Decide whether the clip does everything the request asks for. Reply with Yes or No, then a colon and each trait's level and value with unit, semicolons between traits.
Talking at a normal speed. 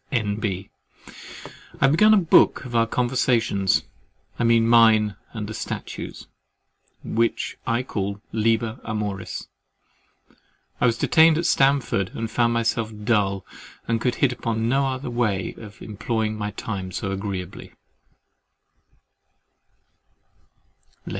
No: slow, 115 wpm